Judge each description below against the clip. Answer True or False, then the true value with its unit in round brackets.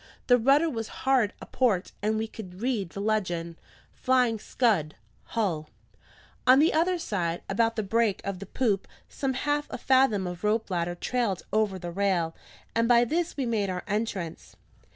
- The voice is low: False (215 Hz)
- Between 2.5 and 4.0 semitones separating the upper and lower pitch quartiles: False (4.9 semitones)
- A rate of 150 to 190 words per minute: True (170 wpm)